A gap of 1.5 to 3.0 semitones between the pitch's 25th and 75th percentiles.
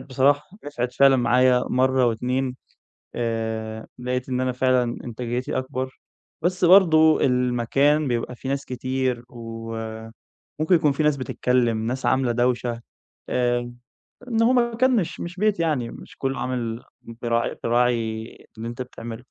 Yes: average, 2.7 semitones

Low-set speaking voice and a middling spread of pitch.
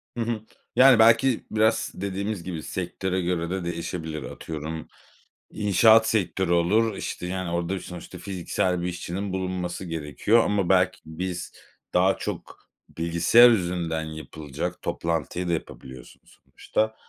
Yes: very low, 90 Hz; average, 3.0 semitones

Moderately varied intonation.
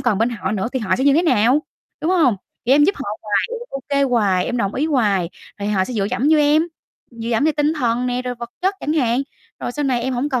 Yes: average, 4.5 semitones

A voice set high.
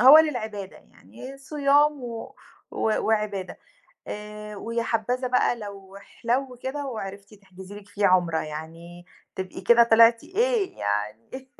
Yes: high, 215 Hz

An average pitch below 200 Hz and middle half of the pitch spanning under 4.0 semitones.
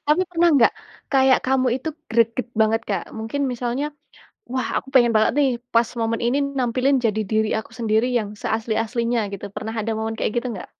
No: high, 235 Hz; average, 2.9 semitones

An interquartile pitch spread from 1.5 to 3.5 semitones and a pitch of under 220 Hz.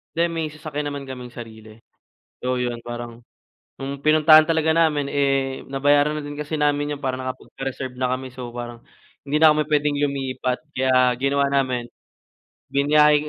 Yes: average, 2.7 semitones; medium, 140 Hz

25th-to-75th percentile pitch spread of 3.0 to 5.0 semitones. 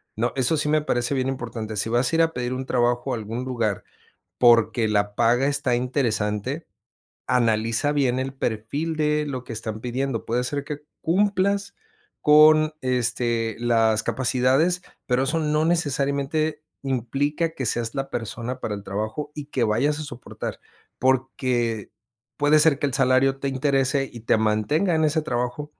Yes: average, 4.0 semitones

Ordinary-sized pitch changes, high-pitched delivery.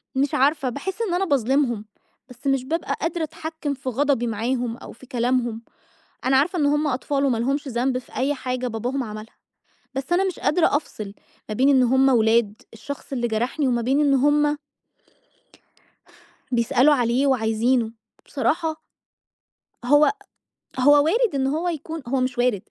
Yes: average, 3.3 semitones; very high, 265 Hz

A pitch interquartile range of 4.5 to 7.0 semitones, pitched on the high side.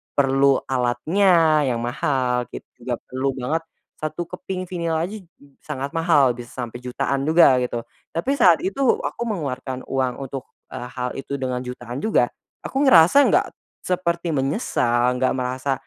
No: average, 5.0 semitones; low, 135 Hz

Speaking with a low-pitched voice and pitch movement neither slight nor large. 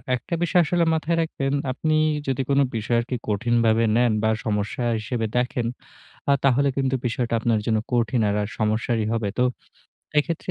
Yes: low, 120 Hz; average, 3.4 semitones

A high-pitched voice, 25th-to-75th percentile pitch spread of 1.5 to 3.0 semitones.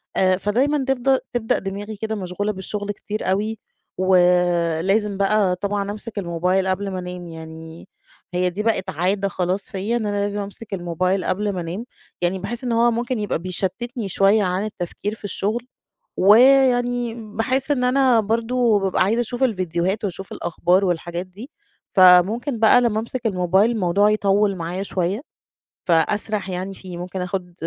No: high, 200 Hz; average, 3.5 semitones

